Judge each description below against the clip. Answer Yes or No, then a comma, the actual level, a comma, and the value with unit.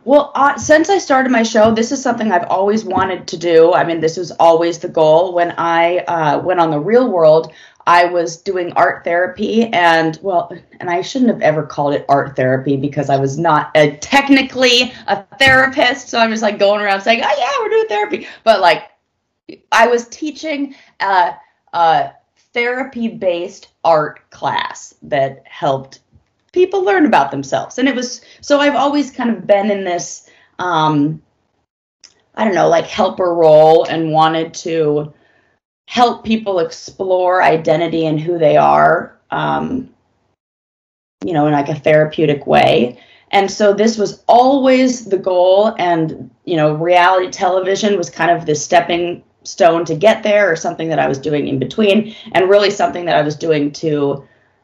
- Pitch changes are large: Yes, wide, 6.2 semitones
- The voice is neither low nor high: Yes, medium, 180 Hz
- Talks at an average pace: Yes, average, 170 wpm